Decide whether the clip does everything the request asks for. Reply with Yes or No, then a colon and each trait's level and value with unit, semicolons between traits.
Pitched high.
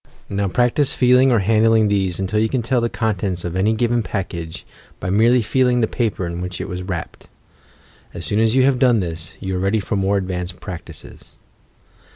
No: low, 105 Hz